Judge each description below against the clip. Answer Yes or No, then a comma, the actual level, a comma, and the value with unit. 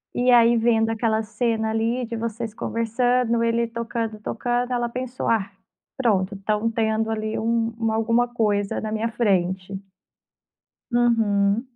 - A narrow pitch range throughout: Yes, narrow, 1.5 semitones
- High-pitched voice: Yes, high, 225 Hz